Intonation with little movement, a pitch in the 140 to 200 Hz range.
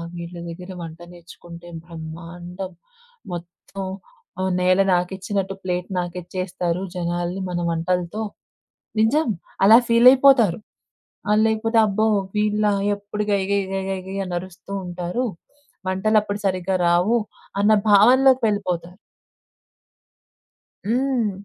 No: average, 3.2 semitones; high, 190 Hz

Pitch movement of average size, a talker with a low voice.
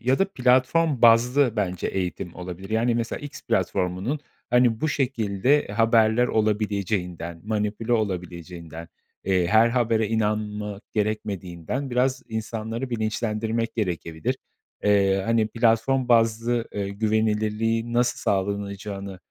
Yes: average, 3.0 semitones; low, 110 Hz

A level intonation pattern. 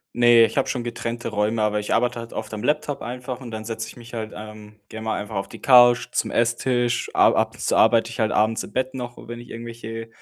Yes: narrow, 1.9 semitones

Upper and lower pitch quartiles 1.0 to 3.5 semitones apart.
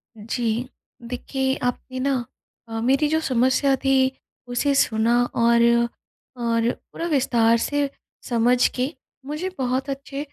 Yes: narrow, 2.6 semitones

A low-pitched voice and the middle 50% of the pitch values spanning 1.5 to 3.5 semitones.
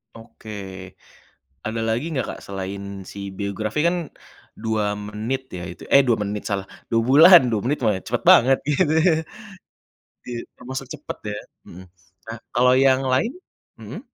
No: low, 115 Hz; average, 4.6 semitones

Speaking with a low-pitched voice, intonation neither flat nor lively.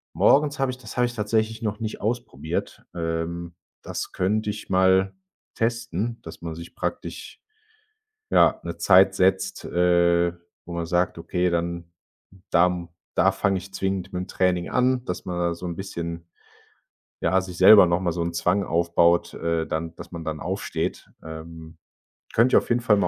Yes: very low, 90 Hz; average, 3.1 semitones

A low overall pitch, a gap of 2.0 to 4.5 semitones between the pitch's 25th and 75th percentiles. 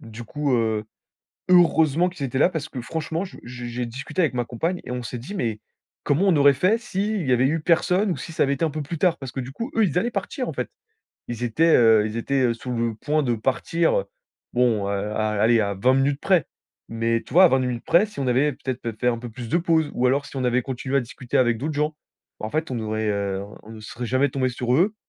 No: low, 130 Hz; average, 5.3 semitones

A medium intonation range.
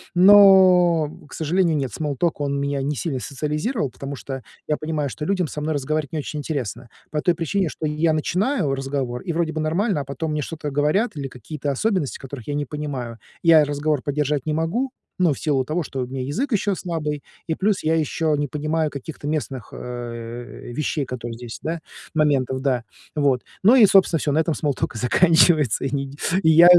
Yes: average, 3.2 semitones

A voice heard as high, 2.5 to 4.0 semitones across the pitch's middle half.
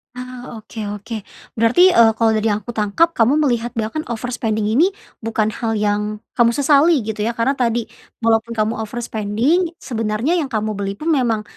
Yes: high, 230 Hz; average, 2.8 semitones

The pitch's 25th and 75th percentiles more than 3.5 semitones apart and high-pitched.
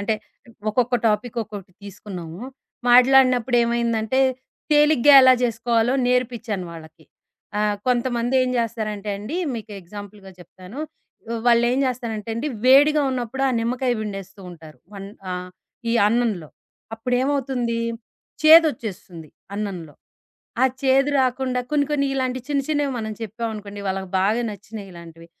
Yes: average, 4.0 semitones; high, 230 Hz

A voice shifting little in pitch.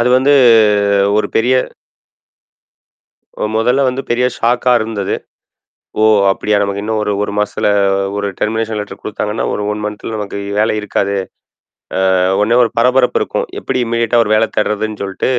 Yes: narrow, 2.3 semitones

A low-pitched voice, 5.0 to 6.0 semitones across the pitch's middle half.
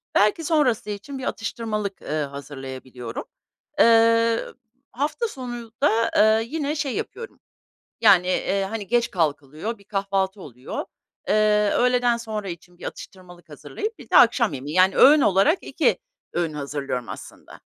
No: high, 210 Hz; wide, 5.4 semitones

